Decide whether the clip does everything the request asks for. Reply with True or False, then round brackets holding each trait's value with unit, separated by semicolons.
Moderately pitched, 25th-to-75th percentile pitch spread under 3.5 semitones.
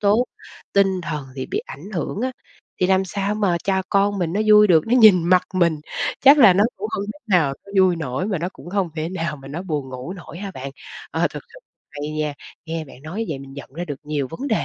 False (180 Hz; 4.7 semitones)